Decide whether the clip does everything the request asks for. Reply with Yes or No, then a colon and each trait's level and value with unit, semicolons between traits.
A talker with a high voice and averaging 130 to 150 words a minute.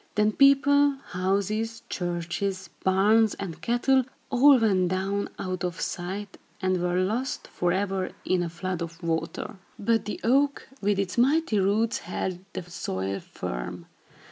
Yes: high, 195 Hz; average, 140 wpm